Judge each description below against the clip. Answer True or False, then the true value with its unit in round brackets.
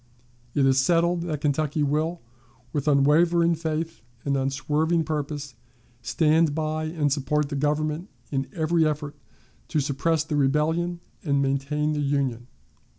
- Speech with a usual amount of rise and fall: False (2.3 semitones)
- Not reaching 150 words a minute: True (135 wpm)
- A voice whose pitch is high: False (150 Hz)